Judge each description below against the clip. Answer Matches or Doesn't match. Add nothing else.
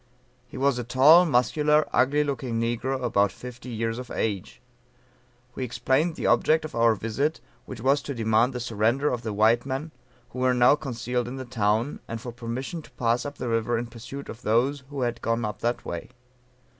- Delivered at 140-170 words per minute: Doesn't match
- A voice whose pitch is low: Matches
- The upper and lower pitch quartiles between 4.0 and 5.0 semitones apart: Doesn't match